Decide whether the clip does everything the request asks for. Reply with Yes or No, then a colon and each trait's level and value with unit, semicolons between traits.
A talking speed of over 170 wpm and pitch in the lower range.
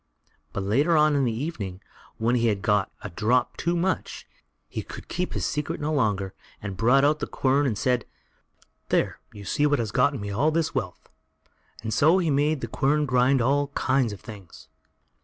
Yes: average, 195 wpm; low, 130 Hz